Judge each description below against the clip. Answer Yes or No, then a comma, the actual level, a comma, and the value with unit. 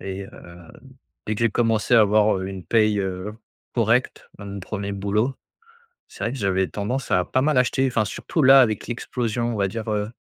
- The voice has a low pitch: Yes, low, 105 Hz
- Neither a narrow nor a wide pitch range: Yes, average, 3.2 semitones